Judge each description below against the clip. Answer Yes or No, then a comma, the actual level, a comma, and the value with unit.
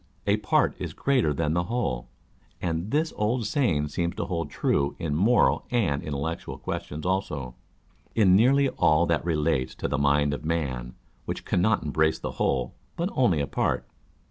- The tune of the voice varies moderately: No, wide, 6.4 semitones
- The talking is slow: No, average, 170 wpm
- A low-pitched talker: Yes, very low, 85 Hz